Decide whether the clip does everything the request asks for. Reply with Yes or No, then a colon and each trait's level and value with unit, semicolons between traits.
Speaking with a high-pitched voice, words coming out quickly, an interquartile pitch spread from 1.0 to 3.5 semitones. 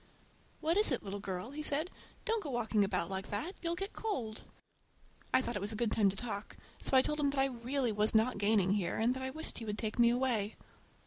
No: high, 235 Hz; fast, 240 wpm; average, 5.2 semitones